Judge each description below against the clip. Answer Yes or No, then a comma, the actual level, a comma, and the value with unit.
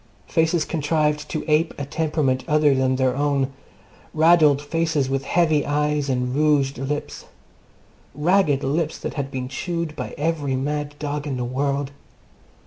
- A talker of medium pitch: Yes, medium, 145 Hz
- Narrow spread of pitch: Yes, narrow, 2.3 semitones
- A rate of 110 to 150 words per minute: Yes, average, 145 wpm